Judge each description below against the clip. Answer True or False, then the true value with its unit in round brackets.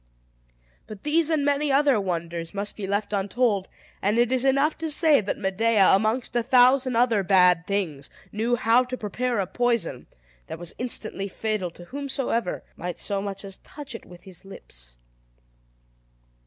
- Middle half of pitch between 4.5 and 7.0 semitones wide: True (4.8 semitones)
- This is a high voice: True (215 Hz)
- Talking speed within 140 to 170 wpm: True (165 wpm)